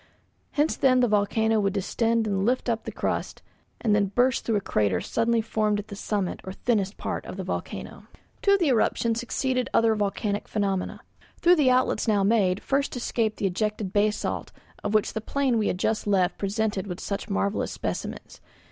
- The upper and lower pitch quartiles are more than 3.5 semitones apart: No, average, 2.7 semitones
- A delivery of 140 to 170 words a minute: No, average, 185 wpm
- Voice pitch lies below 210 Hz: No, high, 215 Hz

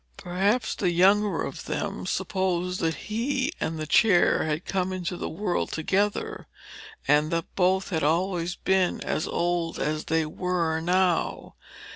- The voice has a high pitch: No, medium, 180 Hz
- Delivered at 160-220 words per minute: No, average, 145 wpm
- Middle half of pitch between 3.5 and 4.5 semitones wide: No, average, 2.7 semitones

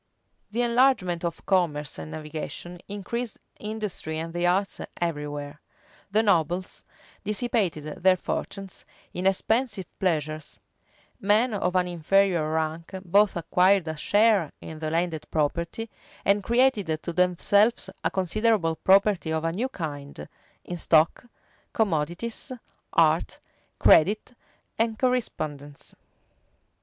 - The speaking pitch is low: No, medium, 180 Hz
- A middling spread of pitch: Yes, average, 4.7 semitones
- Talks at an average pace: No, slow, 115 wpm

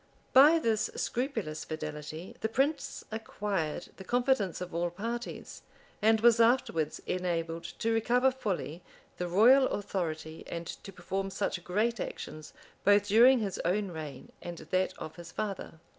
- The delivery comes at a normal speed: Yes, average, 145 wpm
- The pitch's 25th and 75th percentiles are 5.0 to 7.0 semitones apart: Yes, wide, 5.4 semitones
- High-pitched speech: Yes, high, 195 Hz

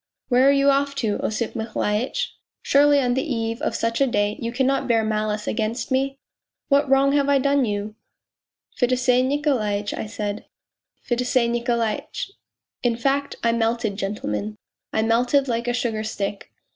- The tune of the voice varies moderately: Yes, average, 3.9 semitones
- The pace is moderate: Yes, average, 180 wpm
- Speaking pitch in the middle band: No, high, 240 Hz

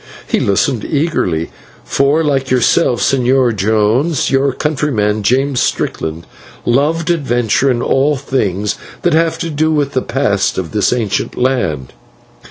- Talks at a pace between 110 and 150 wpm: Yes, slow, 135 wpm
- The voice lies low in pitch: Yes, low, 130 Hz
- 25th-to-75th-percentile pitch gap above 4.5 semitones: Yes, average, 5.2 semitones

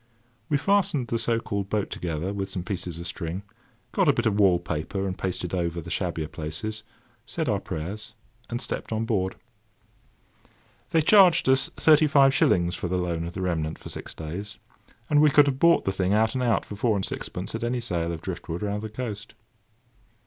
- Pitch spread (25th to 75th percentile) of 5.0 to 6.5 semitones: Yes, wide, 5.4 semitones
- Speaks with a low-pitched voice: Yes, low, 100 Hz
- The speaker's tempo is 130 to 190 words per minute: No, fast, 205 wpm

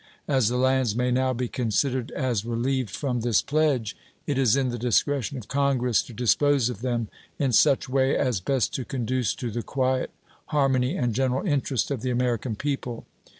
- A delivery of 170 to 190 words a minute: Yes, average, 185 wpm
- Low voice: Yes, low, 125 Hz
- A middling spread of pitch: No, narrow, 2.2 semitones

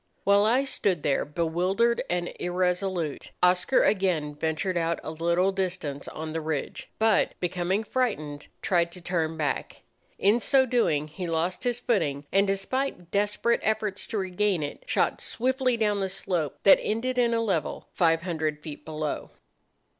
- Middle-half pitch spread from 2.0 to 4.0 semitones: No, average, 4.7 semitones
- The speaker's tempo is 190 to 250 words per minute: No, average, 155 wpm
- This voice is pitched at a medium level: Yes, medium, 180 Hz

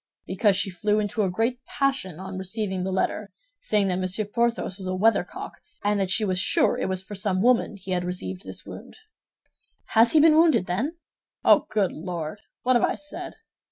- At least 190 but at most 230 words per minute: Yes, average, 195 wpm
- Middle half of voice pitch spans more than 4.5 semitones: No, average, 3.3 semitones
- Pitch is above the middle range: Yes, high, 200 Hz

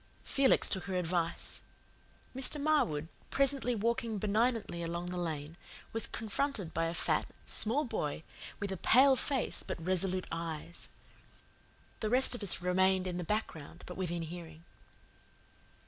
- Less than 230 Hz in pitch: Yes, medium, 185 Hz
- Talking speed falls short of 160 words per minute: Yes, average, 140 wpm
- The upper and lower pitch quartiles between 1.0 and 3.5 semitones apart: No, wide, 5.6 semitones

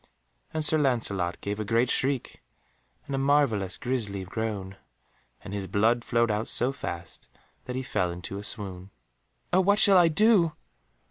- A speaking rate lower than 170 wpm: Yes, average, 160 wpm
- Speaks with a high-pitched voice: No, low, 115 Hz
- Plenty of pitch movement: Yes, wide, 6.0 semitones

